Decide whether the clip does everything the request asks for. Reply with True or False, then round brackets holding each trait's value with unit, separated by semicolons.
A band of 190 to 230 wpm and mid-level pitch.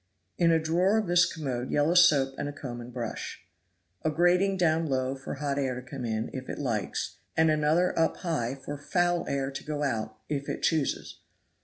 True (200 wpm; 145 Hz)